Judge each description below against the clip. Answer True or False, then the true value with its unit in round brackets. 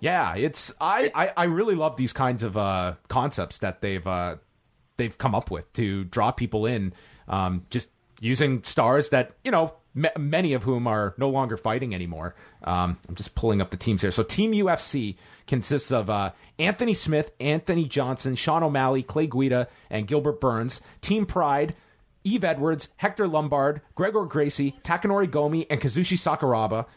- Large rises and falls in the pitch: True (6.5 semitones)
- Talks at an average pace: True (170 wpm)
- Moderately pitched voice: False (130 Hz)